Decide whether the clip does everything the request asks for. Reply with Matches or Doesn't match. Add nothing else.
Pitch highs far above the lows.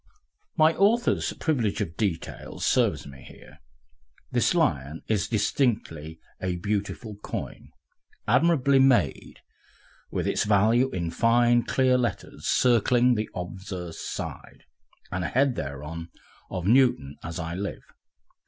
Matches